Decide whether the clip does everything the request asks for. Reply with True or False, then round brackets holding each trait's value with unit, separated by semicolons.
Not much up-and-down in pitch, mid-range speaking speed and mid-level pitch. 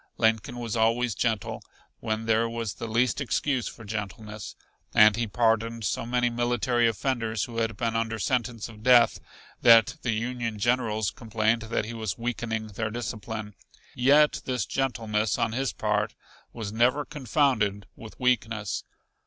False (1.9 semitones; 150 wpm; 115 Hz)